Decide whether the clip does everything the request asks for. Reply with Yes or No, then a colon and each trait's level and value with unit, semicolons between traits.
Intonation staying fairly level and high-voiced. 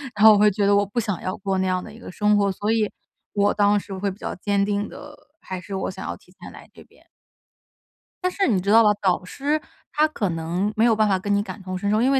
Yes: narrow, 2.1 semitones; high, 205 Hz